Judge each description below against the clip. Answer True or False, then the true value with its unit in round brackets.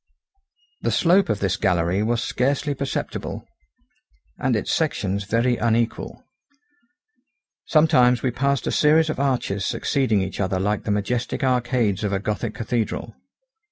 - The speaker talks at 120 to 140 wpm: True (135 wpm)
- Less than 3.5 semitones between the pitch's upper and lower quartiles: False (4.8 semitones)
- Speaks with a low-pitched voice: True (120 Hz)